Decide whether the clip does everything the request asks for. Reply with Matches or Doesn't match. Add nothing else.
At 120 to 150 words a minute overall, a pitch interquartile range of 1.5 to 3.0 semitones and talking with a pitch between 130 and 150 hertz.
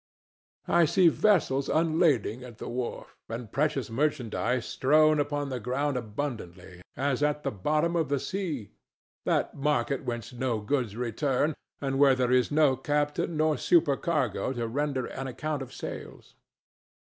Doesn't match